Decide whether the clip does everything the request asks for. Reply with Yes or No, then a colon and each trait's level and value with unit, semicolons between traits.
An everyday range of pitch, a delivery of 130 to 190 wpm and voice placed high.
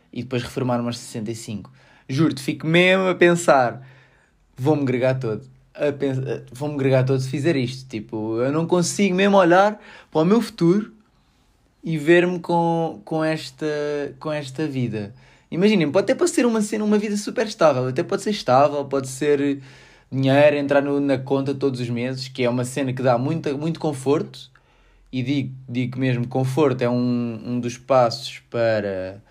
No: average, 4.7 semitones; average, 170 wpm; medium, 140 Hz